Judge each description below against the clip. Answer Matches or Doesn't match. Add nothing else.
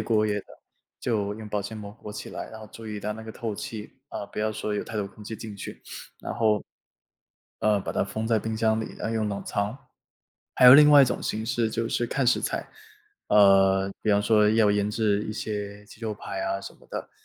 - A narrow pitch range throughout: Matches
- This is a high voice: Doesn't match